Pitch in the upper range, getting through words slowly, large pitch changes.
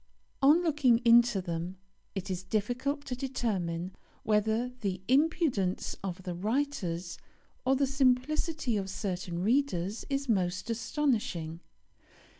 Yes: high, 225 Hz; slow, 115 wpm; wide, 6.5 semitones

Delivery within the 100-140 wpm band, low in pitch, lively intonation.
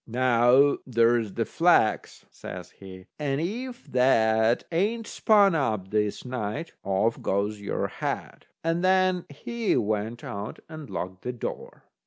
Yes: slow, 135 wpm; low, 125 Hz; wide, 7.6 semitones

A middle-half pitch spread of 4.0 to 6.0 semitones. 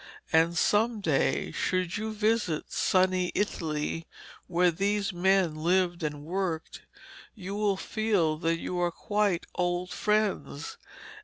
No: average, 3.6 semitones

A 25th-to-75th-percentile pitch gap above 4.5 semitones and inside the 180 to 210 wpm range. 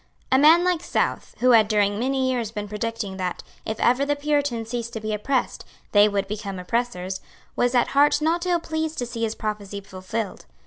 Yes: average, 4.9 semitones; average, 195 wpm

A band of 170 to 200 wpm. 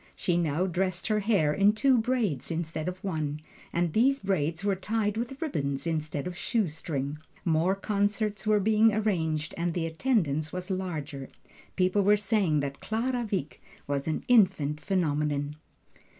No: average, 160 wpm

